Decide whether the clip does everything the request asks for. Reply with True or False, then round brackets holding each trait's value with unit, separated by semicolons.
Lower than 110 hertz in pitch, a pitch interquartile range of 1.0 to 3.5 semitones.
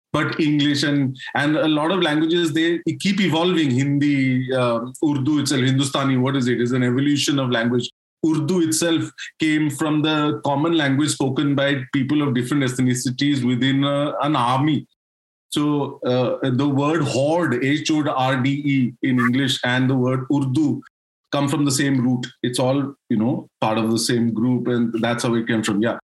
False (140 Hz; 3.0 semitones)